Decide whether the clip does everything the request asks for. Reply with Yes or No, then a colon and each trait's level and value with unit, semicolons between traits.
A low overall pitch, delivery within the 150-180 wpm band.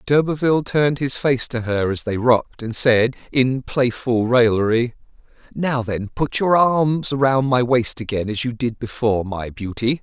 Yes: low, 125 Hz; average, 175 wpm